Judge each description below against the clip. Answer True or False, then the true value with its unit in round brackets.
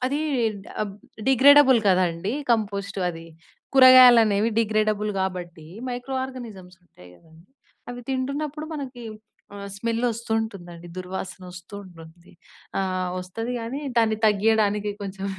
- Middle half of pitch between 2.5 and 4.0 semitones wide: False (4.8 semitones)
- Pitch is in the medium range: False (210 Hz)